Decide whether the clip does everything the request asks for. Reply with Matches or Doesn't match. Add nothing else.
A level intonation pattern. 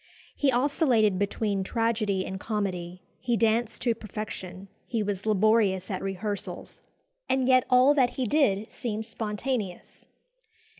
Doesn't match